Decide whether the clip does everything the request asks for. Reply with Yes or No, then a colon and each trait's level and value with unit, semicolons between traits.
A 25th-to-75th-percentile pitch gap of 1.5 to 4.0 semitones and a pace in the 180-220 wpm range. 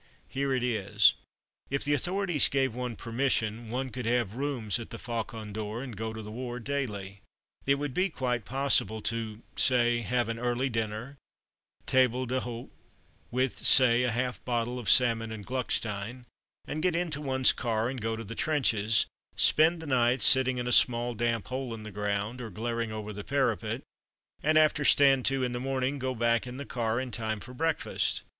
Yes: average, 2.7 semitones; average, 185 wpm